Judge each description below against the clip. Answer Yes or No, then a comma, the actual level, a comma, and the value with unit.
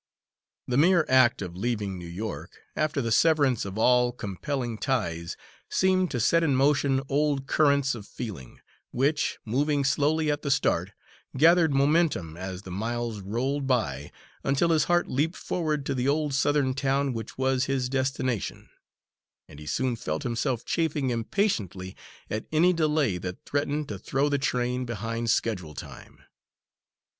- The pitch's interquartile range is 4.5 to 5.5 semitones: Yes, average, 4.8 semitones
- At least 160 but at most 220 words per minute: No, average, 150 wpm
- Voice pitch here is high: No, low, 130 Hz